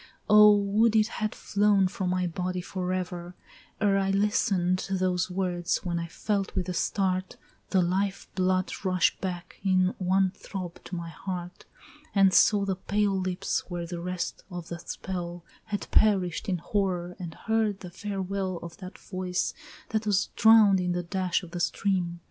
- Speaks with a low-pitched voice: No, medium, 185 Hz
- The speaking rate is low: No, average, 165 wpm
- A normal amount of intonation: No, narrow, 1.9 semitones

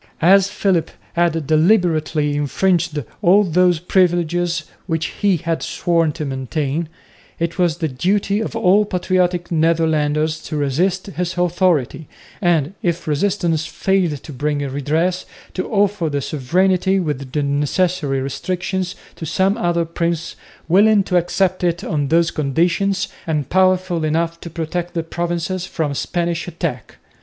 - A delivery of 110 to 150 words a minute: Yes, slow, 135 wpm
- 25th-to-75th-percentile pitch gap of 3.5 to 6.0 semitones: No, average, 2.9 semitones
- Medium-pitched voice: Yes, medium, 170 Hz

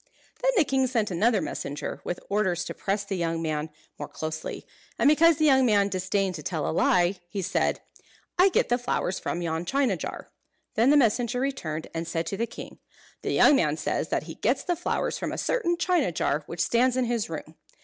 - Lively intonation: Yes, wide, 7.5 semitones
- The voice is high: Yes, high, 200 Hz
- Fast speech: Yes, fast, 210 wpm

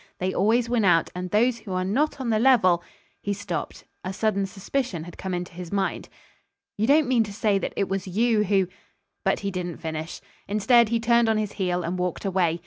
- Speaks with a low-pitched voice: No, high, 200 Hz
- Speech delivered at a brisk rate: Yes, fast, 225 wpm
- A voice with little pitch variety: No, average, 3.8 semitones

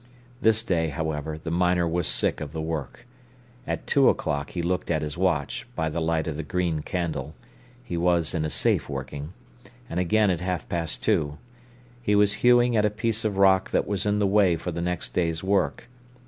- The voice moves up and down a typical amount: Yes, average, 4.3 semitones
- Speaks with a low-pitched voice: Yes, very low, 90 Hz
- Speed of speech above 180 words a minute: Yes, average, 195 wpm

